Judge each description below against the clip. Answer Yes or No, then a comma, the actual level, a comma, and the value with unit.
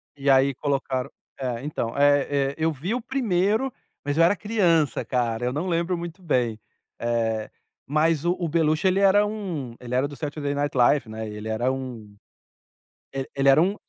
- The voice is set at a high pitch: No, medium, 145 Hz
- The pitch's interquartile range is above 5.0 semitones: Yes, wide, 5.4 semitones